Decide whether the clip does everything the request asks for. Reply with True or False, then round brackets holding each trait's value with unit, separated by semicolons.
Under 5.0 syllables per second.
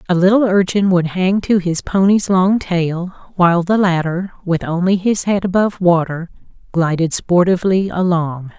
True (4.7 syllables/s)